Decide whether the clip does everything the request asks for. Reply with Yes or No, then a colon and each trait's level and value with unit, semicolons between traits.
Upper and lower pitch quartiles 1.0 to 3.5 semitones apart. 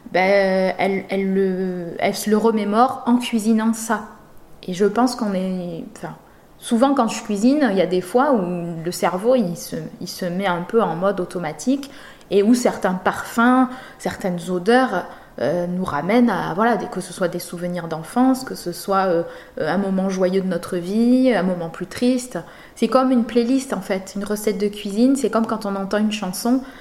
No: average, 4.7 semitones